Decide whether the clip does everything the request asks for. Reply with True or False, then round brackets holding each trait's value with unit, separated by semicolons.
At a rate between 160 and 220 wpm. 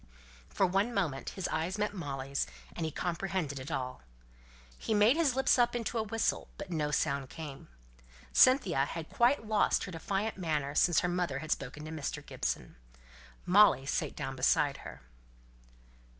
True (165 wpm)